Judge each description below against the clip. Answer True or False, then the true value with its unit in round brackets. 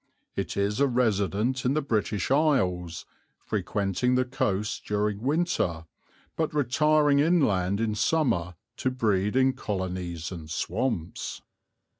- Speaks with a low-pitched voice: True (110 Hz)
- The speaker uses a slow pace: True (120 wpm)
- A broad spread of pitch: True (5.9 semitones)